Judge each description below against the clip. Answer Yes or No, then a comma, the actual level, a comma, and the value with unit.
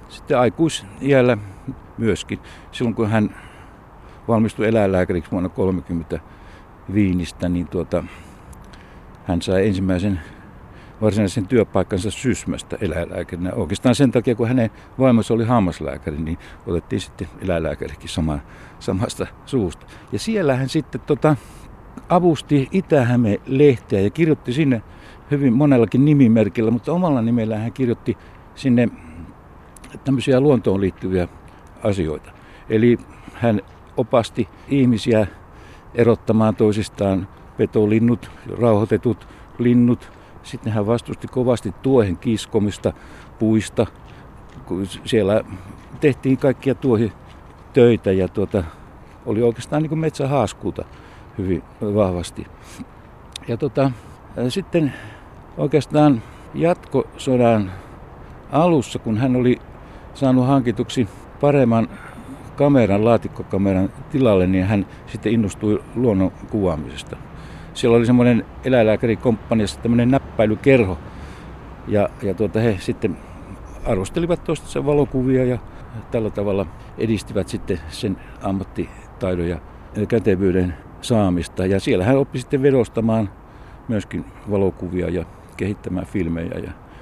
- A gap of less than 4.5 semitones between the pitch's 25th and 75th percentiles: No, average, 5.1 semitones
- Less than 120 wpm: Yes, average, 100 wpm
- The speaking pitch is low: Yes, low, 110 Hz